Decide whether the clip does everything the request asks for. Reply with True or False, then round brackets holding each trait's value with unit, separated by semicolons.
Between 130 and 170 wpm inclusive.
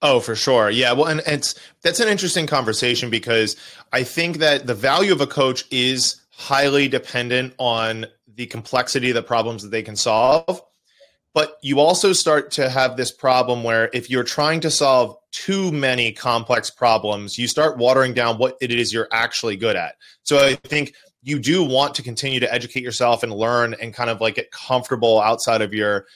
False (195 wpm)